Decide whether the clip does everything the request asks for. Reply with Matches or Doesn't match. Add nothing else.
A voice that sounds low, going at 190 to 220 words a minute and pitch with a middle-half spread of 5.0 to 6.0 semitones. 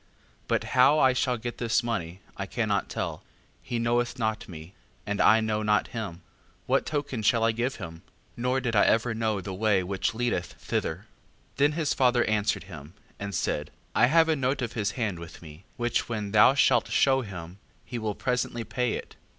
Doesn't match